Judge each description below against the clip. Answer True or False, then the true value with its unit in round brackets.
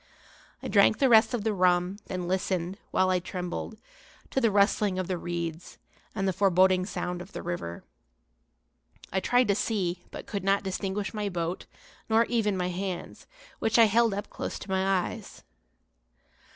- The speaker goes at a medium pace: True (170 wpm)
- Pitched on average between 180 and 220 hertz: True (190 Hz)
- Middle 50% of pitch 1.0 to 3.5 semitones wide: True (2.5 semitones)